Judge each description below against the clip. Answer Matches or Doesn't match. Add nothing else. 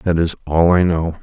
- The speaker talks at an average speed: Doesn't match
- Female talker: Doesn't match